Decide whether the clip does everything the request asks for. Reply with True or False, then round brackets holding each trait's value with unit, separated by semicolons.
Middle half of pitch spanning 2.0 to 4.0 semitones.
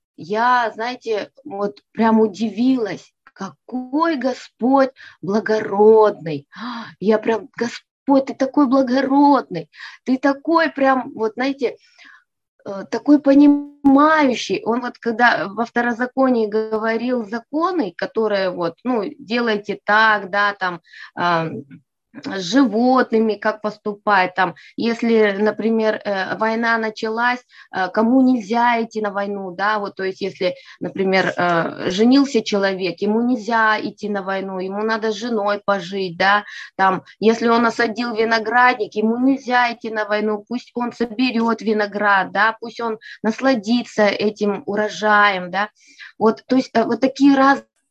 True (3.3 semitones)